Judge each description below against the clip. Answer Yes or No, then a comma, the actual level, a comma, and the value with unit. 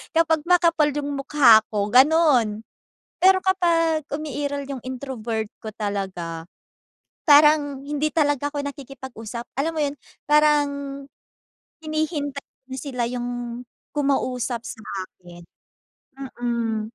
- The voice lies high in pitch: Yes, very high, 280 Hz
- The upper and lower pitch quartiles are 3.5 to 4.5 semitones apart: Yes, average, 4.2 semitones